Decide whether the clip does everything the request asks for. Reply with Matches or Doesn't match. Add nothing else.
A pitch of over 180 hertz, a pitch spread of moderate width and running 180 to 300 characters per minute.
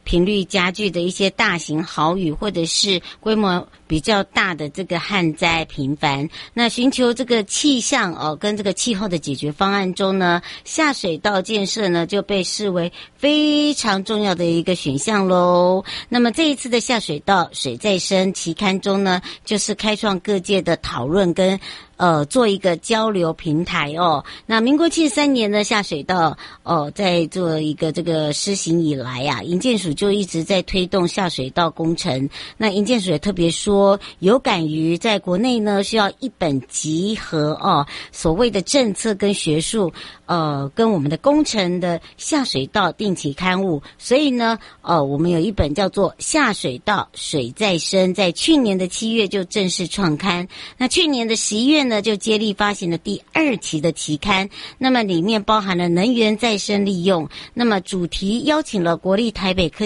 Matches